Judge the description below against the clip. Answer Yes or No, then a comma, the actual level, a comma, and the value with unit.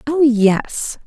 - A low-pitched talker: No, very high, 260 Hz